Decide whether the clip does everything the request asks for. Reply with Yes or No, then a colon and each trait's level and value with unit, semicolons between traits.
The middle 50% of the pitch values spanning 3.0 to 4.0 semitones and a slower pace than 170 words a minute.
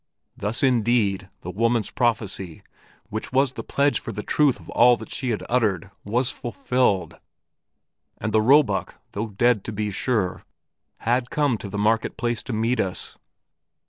Yes: average, 3.3 semitones; average, 160 wpm